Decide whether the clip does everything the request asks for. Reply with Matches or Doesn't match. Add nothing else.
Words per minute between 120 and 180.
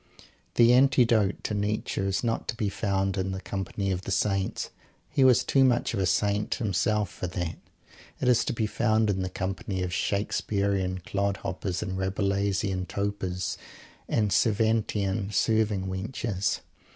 Matches